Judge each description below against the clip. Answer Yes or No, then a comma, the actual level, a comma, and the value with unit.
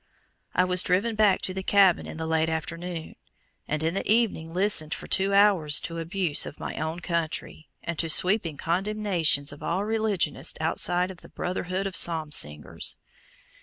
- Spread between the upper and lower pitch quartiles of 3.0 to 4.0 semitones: Yes, average, 3.4 semitones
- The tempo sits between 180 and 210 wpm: No, average, 170 wpm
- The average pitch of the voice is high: No, medium, 175 Hz